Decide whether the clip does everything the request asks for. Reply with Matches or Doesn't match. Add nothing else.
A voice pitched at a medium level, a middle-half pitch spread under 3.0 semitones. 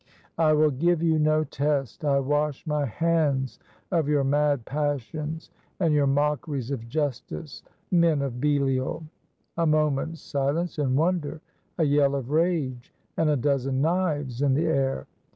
Matches